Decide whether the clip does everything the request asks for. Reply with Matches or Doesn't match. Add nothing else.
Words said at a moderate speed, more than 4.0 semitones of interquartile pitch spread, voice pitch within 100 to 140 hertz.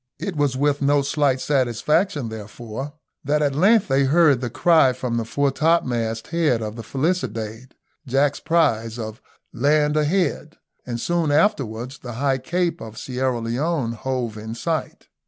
Matches